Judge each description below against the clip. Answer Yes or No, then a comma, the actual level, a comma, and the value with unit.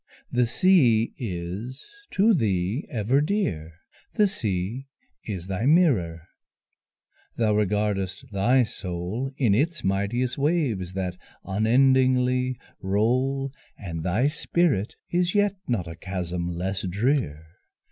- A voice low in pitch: Yes, low, 110 Hz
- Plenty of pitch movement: Yes, wide, 6.3 semitones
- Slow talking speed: Yes, slow, 110 wpm